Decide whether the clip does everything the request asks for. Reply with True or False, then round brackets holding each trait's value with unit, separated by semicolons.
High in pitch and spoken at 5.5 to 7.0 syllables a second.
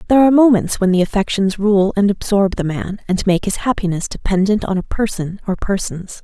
True (195 Hz; 5.7 syllables/s)